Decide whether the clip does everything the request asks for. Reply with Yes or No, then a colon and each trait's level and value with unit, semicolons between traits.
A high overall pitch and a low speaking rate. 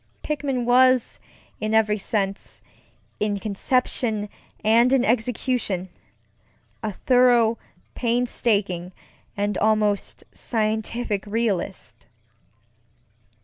Yes: high, 220 Hz; slow, 65 wpm